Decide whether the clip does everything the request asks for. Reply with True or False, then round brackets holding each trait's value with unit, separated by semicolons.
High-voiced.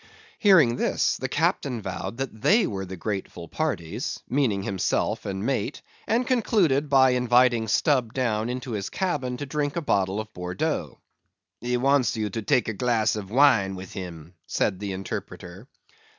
False (115 Hz)